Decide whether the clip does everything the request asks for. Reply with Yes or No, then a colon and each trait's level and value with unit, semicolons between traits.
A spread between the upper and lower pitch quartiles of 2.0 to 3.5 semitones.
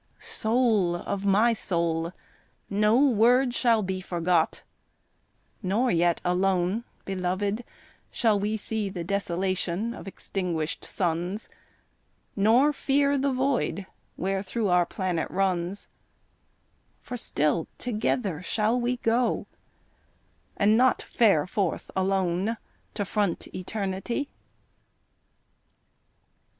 No: average, 4.2 semitones